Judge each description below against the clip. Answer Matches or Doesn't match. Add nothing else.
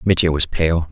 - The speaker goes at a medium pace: Matches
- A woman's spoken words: Doesn't match